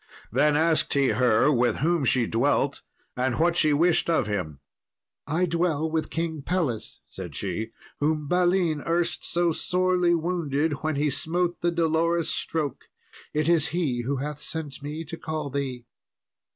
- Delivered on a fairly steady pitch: No, average, 3.4 semitones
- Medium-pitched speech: Yes, medium, 155 Hz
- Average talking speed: Yes, average, 155 wpm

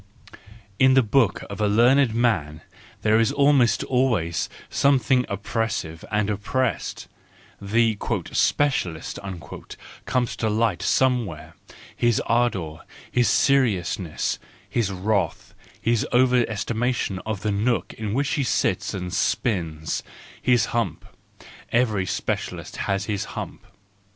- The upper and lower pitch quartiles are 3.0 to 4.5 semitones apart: Yes, average, 4.1 semitones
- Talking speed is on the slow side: Yes, slow, 120 wpm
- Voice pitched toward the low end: Yes, low, 110 Hz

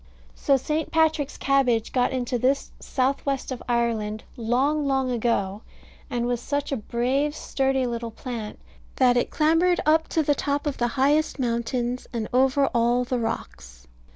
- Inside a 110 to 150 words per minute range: No, average, 160 wpm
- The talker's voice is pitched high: Yes, very high, 255 Hz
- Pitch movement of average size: Yes, average, 3.0 semitones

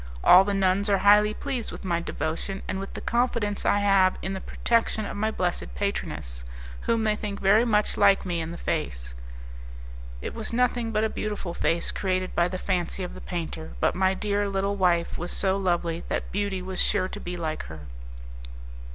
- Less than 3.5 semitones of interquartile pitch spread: Yes, average, 2.9 semitones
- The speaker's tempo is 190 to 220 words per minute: Yes, average, 195 wpm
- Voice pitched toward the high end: Yes, high, 195 Hz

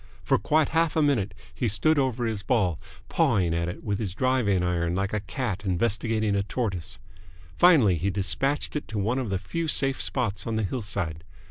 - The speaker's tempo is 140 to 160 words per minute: No, average, 195 wpm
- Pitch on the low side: Yes, low, 105 Hz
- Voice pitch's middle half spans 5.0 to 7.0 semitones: Yes, average, 5.3 semitones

